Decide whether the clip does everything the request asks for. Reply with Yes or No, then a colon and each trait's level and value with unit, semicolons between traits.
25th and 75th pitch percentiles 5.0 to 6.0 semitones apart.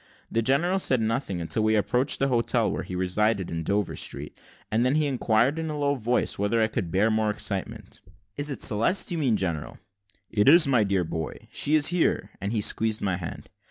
Yes: wide, 5.4 semitones